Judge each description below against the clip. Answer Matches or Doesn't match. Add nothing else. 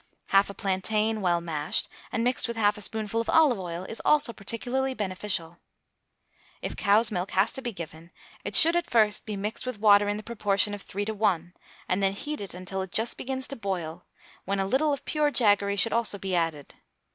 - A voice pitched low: Doesn't match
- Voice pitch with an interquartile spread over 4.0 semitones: Doesn't match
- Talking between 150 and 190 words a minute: Doesn't match